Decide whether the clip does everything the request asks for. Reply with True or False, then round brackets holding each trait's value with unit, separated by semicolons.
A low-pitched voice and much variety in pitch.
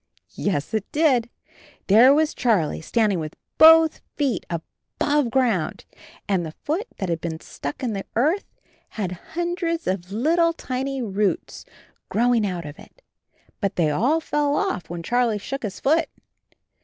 False (235 Hz; 8.0 semitones)